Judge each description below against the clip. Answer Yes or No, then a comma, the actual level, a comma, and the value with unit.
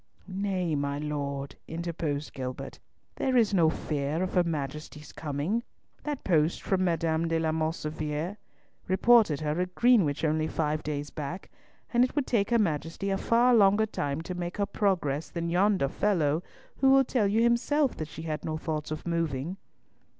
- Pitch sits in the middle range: Yes, medium, 165 Hz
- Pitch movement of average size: Yes, average, 4.9 semitones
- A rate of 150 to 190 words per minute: Yes, average, 170 wpm